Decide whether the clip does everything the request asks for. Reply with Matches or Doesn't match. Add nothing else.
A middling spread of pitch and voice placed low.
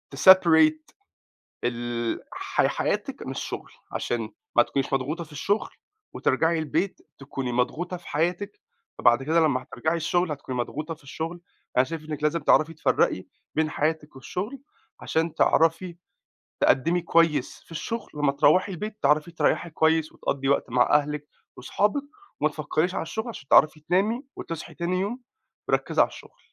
Doesn't match